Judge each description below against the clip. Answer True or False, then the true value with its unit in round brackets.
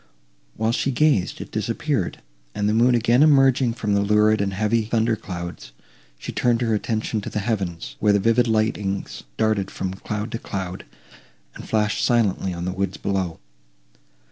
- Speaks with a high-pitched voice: False (105 Hz)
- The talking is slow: False (170 wpm)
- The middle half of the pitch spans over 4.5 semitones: False (3.0 semitones)